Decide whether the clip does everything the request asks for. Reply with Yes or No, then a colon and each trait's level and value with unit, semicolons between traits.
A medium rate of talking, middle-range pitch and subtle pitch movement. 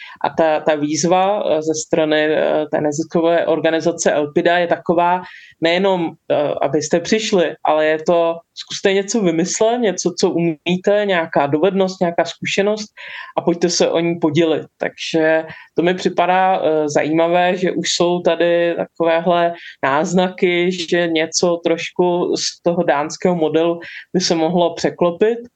Yes: average, 130 wpm; medium, 170 Hz; narrow, 1.9 semitones